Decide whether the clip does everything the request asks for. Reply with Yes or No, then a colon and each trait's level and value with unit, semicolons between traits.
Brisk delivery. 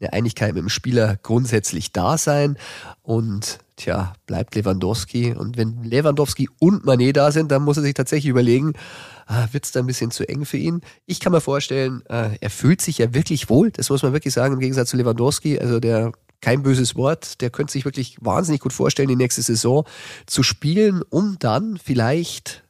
Yes: fast, 195 wpm